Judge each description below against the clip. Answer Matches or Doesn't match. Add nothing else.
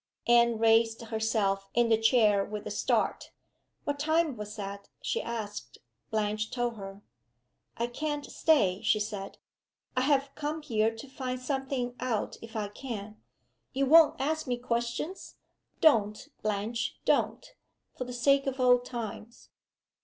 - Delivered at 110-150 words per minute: Matches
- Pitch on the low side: Doesn't match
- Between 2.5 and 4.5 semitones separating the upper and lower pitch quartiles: Matches